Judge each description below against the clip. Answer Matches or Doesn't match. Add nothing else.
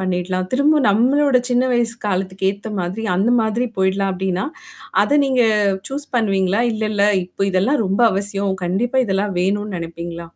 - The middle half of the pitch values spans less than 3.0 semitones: Doesn't match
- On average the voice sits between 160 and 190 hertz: Doesn't match